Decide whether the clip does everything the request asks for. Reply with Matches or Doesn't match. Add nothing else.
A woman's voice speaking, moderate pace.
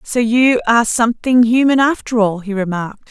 Matches